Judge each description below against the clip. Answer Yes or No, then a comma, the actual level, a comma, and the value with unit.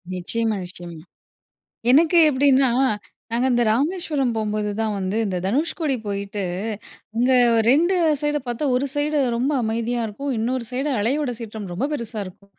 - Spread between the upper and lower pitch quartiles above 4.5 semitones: Yes, average, 4.9 semitones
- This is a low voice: No, high, 240 Hz